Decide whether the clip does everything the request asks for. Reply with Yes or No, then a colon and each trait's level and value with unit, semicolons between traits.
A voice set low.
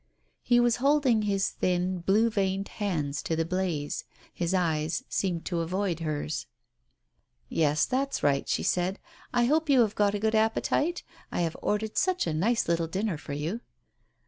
No: high, 190 Hz